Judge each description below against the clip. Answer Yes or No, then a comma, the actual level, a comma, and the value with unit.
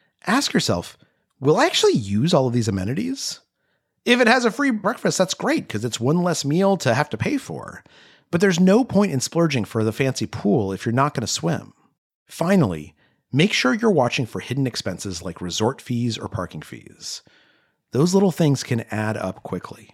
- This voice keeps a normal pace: Yes, average, 195 wpm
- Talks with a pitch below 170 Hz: Yes, low, 135 Hz